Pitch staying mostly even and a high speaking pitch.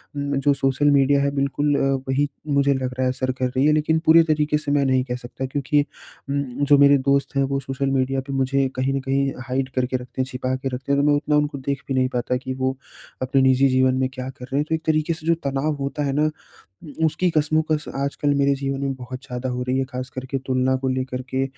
No: narrow, 1.6 semitones; low, 135 Hz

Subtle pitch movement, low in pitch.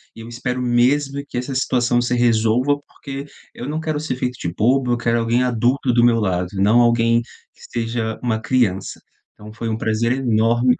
Yes: narrow, 1.9 semitones; low, 120 Hz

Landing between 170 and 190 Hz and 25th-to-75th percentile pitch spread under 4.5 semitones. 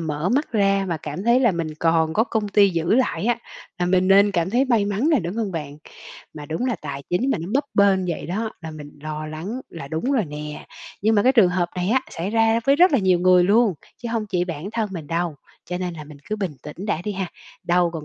No: medium, 185 Hz; average, 5.0 semitones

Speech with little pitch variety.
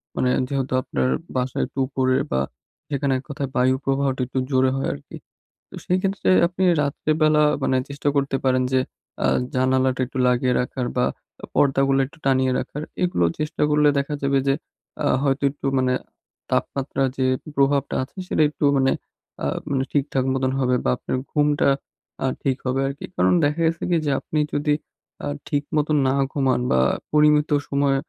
Yes: narrow, 2.0 semitones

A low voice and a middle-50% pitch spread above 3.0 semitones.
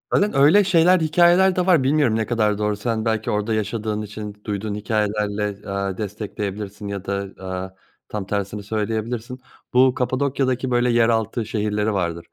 Yes: low, 110 Hz; average, 3.4 semitones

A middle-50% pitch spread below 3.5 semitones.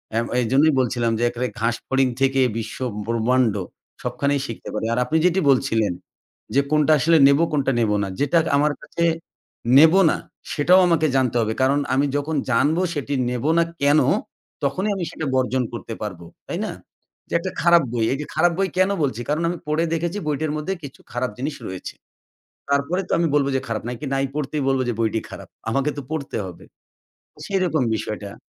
No: average, 4.5 semitones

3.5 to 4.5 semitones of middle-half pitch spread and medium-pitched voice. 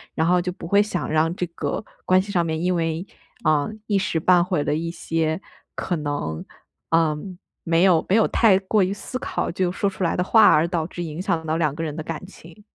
No: average, 2.7 semitones; medium, 170 Hz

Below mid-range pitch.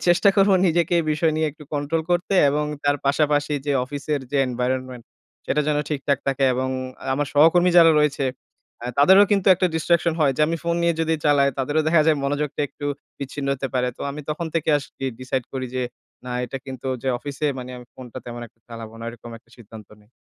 No: medium, 145 Hz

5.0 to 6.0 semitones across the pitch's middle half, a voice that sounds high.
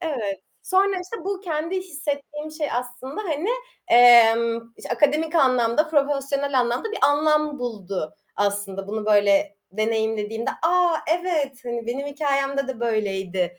Yes: wide, 5.4 semitones; very high, 260 Hz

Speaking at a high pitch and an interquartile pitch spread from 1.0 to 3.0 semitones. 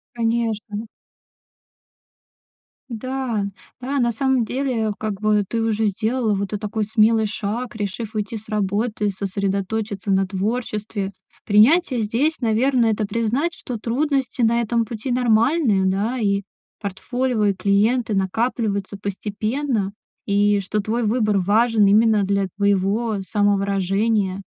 Yes: high, 215 Hz; average, 2.7 semitones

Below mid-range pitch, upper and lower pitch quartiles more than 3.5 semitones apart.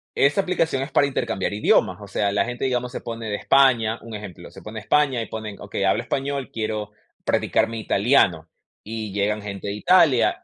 Yes: low, 115 Hz; average, 4.4 semitones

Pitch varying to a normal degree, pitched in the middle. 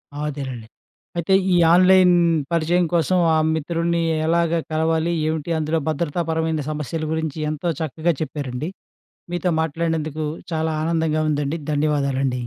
No: narrow, 2.0 semitones; medium, 160 Hz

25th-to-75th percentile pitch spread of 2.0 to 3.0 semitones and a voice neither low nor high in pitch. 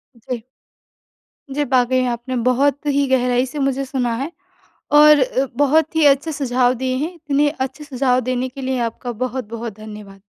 No: narrow, 2.5 semitones; very high, 260 Hz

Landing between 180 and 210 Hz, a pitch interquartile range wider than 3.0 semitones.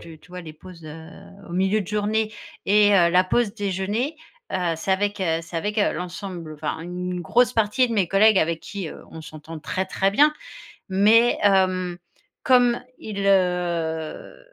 Yes: high, 190 Hz; average, 3.5 semitones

